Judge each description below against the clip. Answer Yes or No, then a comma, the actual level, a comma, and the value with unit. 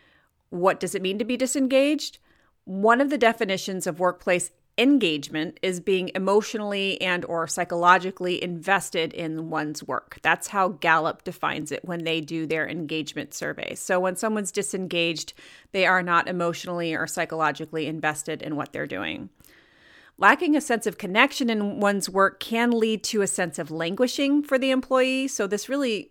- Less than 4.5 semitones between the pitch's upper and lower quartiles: No, average, 4.8 semitones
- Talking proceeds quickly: No, average, 165 wpm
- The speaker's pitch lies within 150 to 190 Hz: Yes, medium, 185 Hz